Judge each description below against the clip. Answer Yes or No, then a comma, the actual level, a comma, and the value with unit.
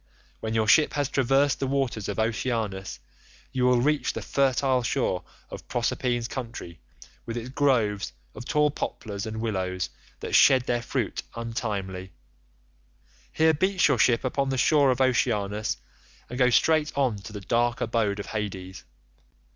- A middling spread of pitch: Yes, average, 4.2 semitones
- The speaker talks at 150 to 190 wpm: Yes, average, 155 wpm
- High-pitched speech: No, low, 120 Hz